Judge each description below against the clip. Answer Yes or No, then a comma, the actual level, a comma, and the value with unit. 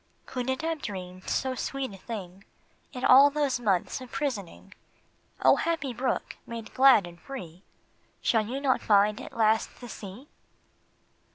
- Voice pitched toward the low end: No, high, 240 Hz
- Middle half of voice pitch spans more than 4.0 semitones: Yes, average, 5.0 semitones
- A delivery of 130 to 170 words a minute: Yes, average, 155 wpm